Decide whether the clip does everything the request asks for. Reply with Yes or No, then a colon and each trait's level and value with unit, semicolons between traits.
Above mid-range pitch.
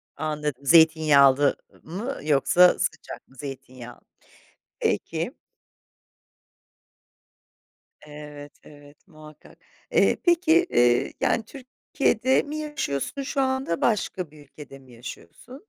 No: medium, 155 Hz